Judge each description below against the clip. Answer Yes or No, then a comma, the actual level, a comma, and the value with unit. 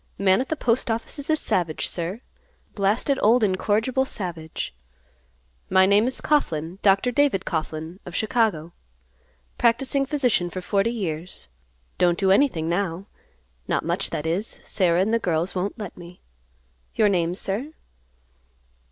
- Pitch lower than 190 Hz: No, high, 195 Hz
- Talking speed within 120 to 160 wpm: Yes, average, 140 wpm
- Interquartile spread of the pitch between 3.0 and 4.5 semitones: No, average, 5.1 semitones